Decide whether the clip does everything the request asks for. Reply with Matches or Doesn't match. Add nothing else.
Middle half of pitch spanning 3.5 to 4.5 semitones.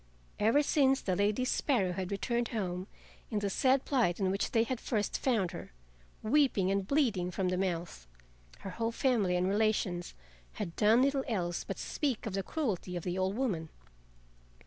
Doesn't match